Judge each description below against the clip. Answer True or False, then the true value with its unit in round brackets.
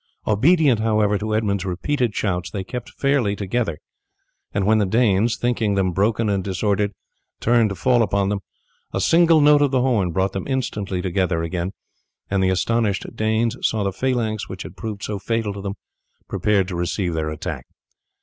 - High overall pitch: False (105 Hz)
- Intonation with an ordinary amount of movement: True (3.4 semitones)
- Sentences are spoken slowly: False (180 wpm)